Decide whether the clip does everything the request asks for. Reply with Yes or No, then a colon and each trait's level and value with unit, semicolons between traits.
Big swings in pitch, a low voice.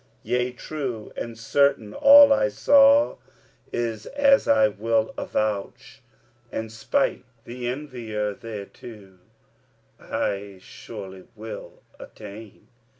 No: average, 4.3 semitones; low, 115 Hz